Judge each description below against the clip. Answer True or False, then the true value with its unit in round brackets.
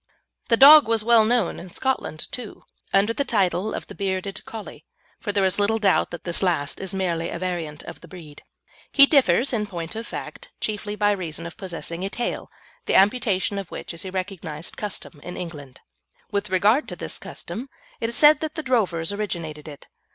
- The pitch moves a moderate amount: True (4.5 semitones)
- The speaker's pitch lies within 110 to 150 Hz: False (195 Hz)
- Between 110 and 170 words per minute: False (195 wpm)